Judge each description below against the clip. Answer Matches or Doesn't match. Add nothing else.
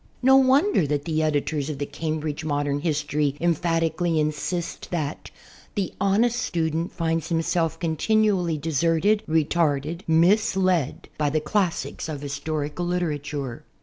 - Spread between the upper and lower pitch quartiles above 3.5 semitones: Doesn't match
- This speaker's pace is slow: Matches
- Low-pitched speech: Doesn't match